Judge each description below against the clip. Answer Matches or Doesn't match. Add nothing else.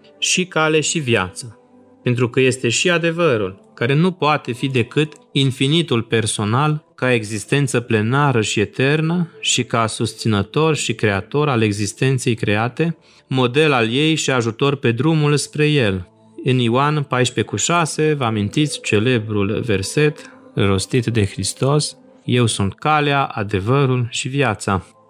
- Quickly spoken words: Doesn't match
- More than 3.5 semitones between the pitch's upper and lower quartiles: Matches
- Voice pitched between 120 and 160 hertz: Matches